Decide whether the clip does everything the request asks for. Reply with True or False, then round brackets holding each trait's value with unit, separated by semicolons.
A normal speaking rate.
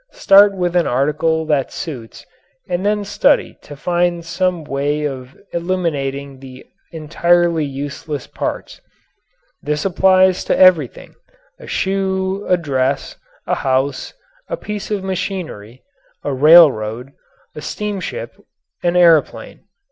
False (115 wpm)